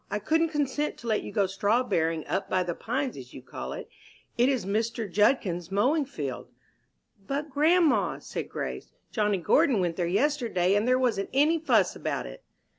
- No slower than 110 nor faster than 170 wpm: No, average, 180 wpm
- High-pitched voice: Yes, high, 225 Hz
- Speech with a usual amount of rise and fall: No, wide, 6.5 semitones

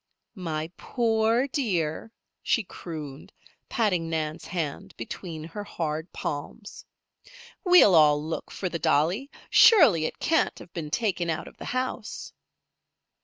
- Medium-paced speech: No, slow, 125 wpm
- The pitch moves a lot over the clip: Yes, wide, 6.1 semitones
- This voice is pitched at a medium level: Yes, medium, 170 Hz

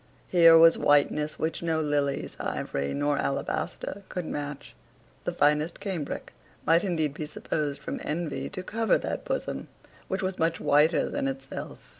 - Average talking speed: Yes, average, 150 wpm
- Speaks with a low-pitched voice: No, medium, 160 Hz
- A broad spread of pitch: No, average, 3.4 semitones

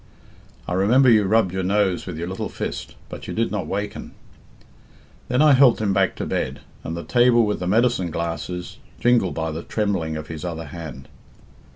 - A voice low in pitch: Yes, very low, 95 Hz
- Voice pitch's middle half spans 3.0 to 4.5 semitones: No, average, 5.1 semitones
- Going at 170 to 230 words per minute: Yes, average, 190 wpm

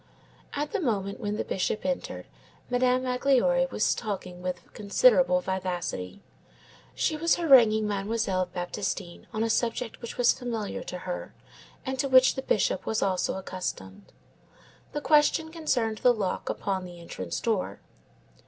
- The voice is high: Yes, high, 215 Hz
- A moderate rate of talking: Yes, average, 145 wpm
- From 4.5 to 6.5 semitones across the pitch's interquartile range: Yes, wide, 5.6 semitones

